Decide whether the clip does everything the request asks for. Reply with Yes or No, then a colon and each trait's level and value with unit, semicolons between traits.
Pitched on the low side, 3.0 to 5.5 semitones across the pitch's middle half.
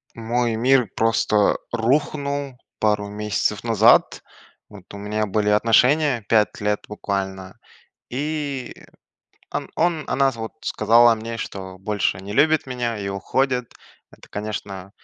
Yes: low, 115 Hz; average, 3.6 semitones